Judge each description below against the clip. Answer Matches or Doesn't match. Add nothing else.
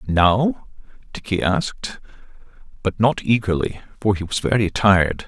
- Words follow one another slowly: Matches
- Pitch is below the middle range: Matches